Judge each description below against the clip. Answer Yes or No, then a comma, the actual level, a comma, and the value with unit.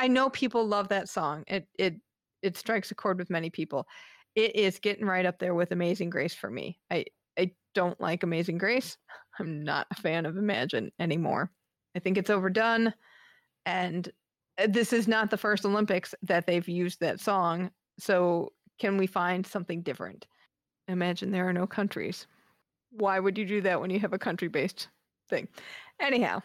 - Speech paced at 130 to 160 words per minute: No, average, 180 wpm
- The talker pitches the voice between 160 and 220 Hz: Yes, high, 190 Hz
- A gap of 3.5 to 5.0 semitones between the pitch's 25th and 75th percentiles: No, average, 3.1 semitones